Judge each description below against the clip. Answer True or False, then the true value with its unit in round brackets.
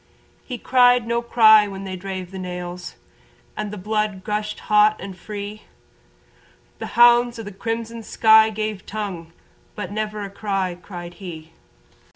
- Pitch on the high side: True (210 Hz)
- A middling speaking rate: True (150 wpm)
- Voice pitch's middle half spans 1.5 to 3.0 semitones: True (2.6 semitones)